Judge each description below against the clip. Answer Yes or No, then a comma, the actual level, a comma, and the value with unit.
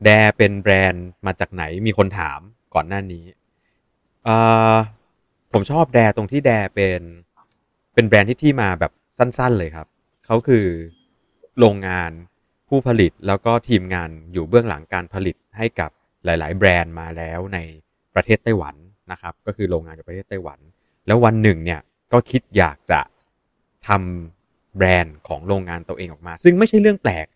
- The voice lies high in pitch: No, very low, 95 Hz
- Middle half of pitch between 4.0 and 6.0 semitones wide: Yes, average, 4.5 semitones